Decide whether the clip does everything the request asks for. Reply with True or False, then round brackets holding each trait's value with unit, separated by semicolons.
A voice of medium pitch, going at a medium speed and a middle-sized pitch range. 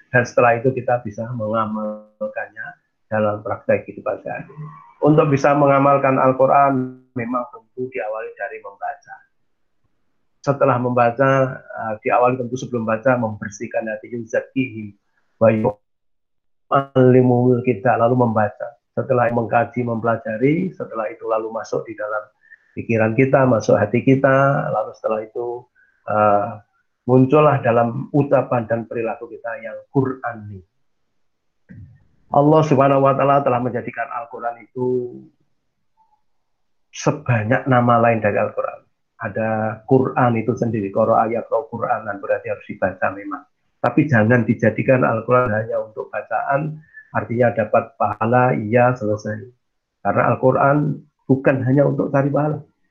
False (125 Hz; 120 wpm; 3.6 semitones)